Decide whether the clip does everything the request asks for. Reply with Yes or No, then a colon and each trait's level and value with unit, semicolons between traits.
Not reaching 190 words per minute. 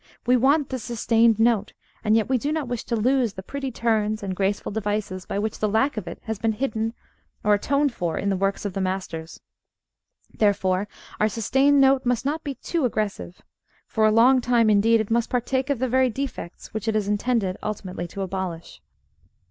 No: average, 200 wpm